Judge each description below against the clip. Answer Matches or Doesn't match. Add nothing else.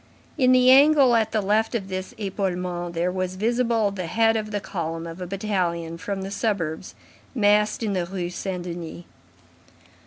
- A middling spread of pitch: Matches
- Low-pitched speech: Doesn't match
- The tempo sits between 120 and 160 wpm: Doesn't match